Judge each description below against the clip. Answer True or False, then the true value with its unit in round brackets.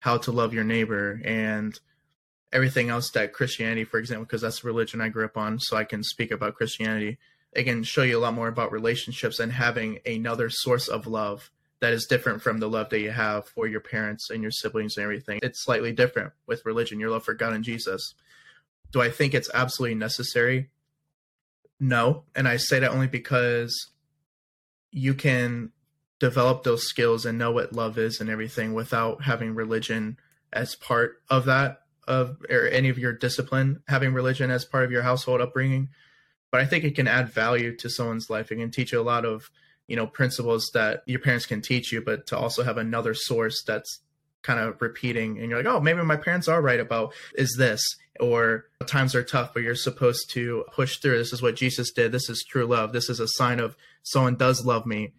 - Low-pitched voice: True (120 Hz)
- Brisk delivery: True (210 wpm)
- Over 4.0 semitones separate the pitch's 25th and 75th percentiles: False (2.4 semitones)